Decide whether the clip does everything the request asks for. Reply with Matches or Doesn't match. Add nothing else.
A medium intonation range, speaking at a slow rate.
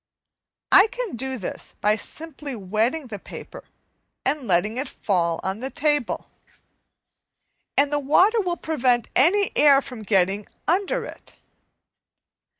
Doesn't match